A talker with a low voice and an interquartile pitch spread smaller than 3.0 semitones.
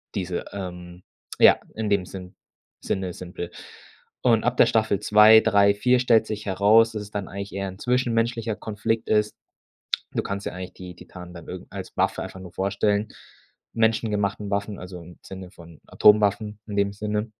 Yes: low, 100 Hz; narrow, 2.6 semitones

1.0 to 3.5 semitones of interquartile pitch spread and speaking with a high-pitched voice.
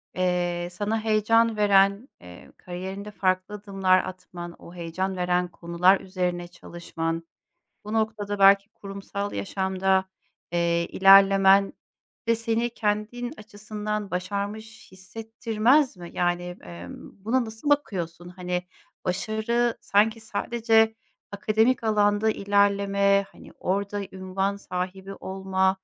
Yes: average, 2.8 semitones; high, 195 Hz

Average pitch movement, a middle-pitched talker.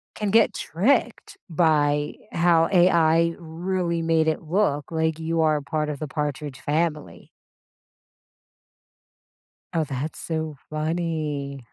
No: narrow, 2.0 semitones; medium, 160 Hz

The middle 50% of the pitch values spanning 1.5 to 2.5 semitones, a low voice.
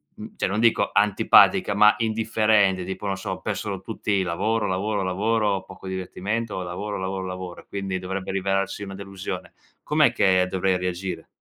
Yes: narrow, 2.0 semitones; very low, 95 Hz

